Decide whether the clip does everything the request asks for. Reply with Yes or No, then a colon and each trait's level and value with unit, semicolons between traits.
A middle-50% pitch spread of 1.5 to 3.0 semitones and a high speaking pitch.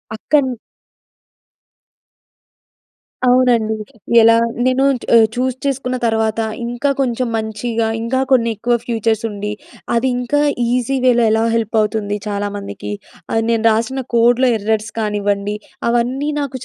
Yes: narrow, 2.5 semitones; high, 230 Hz